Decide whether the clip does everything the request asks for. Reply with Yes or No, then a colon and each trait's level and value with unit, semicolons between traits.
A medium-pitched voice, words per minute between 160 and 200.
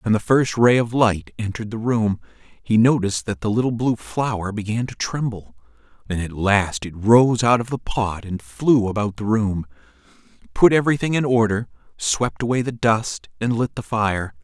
No: low, 110 Hz; average, 185 wpm